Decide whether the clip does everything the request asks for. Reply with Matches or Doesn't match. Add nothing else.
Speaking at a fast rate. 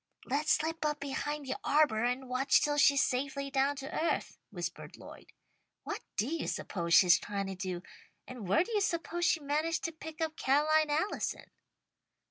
Doesn't match